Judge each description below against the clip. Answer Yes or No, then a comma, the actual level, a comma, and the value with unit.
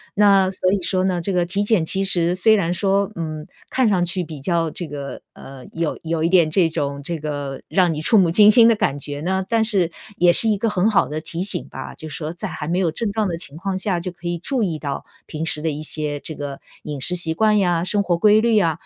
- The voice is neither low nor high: Yes, medium, 175 Hz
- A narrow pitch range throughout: No, average, 3.8 semitones